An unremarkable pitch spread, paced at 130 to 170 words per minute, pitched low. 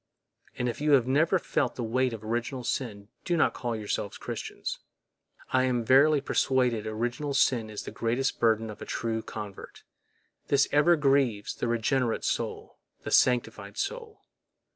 Yes: average, 3.5 semitones; average, 160 wpm; low, 120 Hz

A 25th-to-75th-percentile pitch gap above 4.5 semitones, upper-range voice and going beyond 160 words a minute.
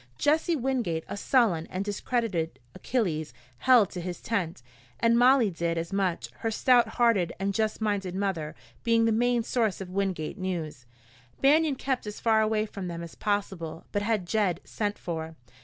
Yes: average, 4.9 semitones; high, 205 Hz; average, 170 wpm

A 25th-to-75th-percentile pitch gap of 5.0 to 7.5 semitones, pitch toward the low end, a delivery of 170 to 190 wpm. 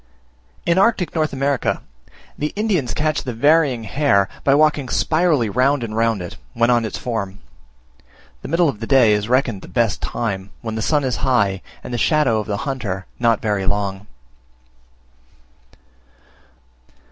No: wide, 5.5 semitones; low, 120 Hz; average, 160 wpm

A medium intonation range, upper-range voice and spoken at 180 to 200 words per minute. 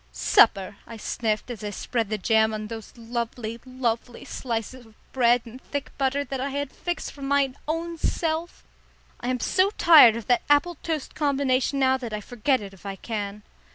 Yes: average, 4.2 semitones; high, 245 Hz; average, 190 wpm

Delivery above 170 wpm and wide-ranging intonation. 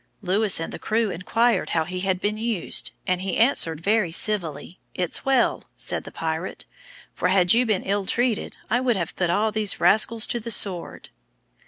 No: average, 185 wpm; average, 3.8 semitones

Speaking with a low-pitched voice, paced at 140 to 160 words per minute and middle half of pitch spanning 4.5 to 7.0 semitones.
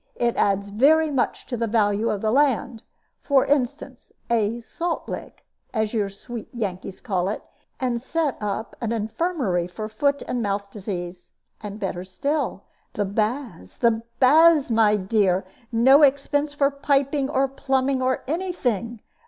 No: high, 235 Hz; average, 155 wpm; average, 5.1 semitones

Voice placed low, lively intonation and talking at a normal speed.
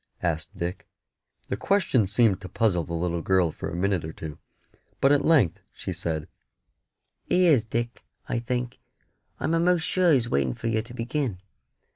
Yes: low, 115 Hz; wide, 7.7 semitones; average, 170 wpm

